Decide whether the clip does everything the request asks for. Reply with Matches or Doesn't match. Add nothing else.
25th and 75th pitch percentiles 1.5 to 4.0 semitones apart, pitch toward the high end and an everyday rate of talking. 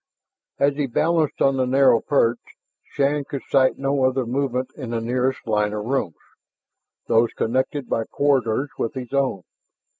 Doesn't match